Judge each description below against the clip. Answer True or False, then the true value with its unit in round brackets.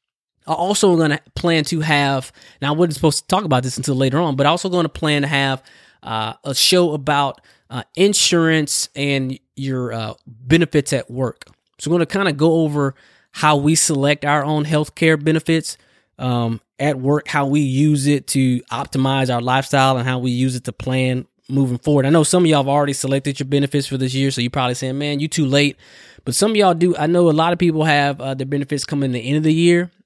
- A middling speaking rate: False (235 wpm)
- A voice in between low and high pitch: True (145 Hz)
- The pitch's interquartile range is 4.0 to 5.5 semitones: False (3.1 semitones)